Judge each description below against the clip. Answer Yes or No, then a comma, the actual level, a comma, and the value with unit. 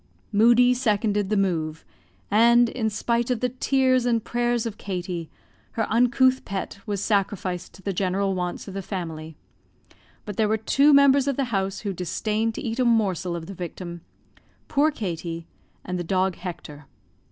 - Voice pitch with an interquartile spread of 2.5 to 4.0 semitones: No, average, 4.7 semitones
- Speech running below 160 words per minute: No, average, 170 wpm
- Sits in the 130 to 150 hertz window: No, high, 205 Hz